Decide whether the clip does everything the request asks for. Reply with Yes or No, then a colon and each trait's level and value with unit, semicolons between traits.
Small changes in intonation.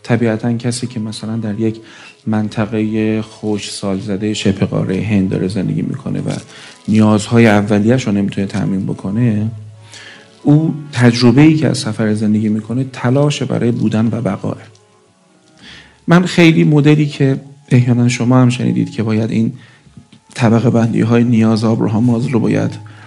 Yes: narrow, 2.3 semitones